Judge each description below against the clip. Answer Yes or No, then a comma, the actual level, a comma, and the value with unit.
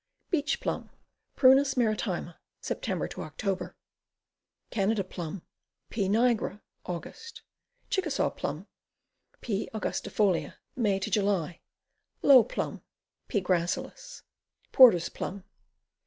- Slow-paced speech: Yes, slow, 85 wpm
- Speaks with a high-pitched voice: Yes, high, 210 Hz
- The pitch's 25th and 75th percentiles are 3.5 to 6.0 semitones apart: Yes, wide, 5.5 semitones